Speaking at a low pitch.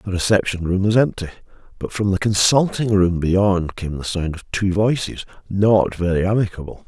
Yes: very low, 95 Hz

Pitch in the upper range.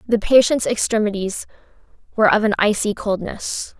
Yes: high, 215 Hz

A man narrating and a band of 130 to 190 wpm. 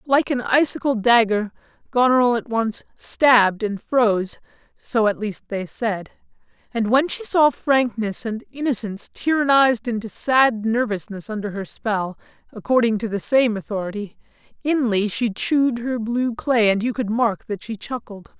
Yes: male; average, 155 wpm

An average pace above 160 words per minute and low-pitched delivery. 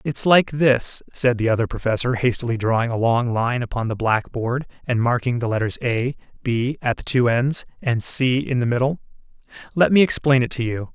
Yes: fast, 205 wpm; low, 125 Hz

